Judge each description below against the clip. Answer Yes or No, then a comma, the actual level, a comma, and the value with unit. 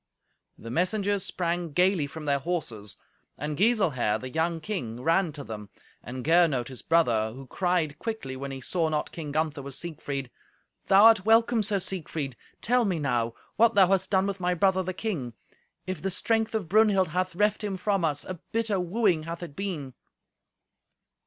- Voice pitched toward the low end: No, medium, 175 Hz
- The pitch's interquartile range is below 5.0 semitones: No, wide, 5.6 semitones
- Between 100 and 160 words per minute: No, average, 180 wpm